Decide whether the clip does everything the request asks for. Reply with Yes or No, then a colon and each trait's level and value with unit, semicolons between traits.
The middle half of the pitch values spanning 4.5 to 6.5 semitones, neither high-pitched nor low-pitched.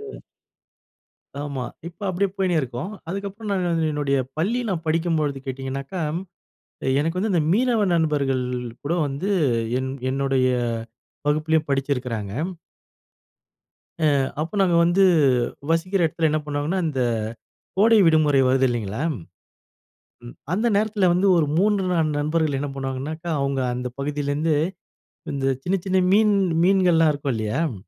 Yes: average, 5.0 semitones; medium, 155 Hz